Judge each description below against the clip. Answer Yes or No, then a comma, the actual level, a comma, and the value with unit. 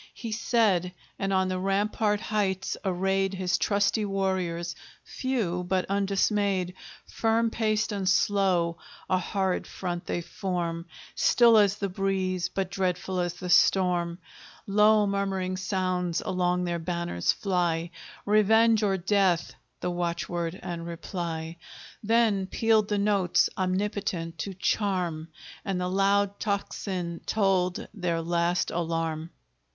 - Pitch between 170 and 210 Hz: Yes, high, 190 Hz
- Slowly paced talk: Yes, slow, 125 wpm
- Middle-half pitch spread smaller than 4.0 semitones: Yes, narrow, 2.5 semitones